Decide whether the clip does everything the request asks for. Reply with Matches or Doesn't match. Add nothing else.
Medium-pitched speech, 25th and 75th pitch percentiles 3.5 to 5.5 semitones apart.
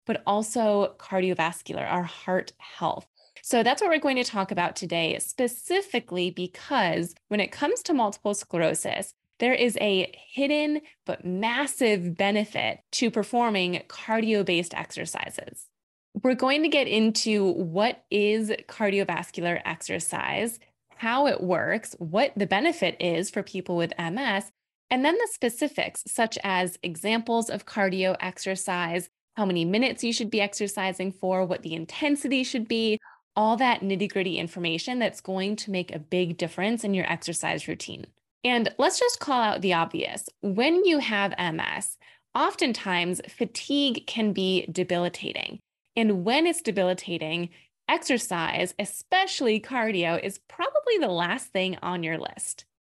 Doesn't match